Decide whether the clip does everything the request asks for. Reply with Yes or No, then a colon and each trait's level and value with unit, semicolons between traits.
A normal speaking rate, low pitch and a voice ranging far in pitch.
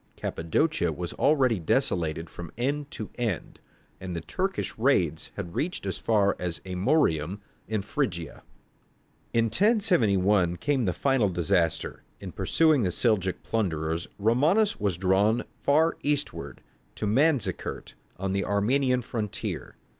No: slow, 125 wpm; low, 105 Hz; wide, 7.4 semitones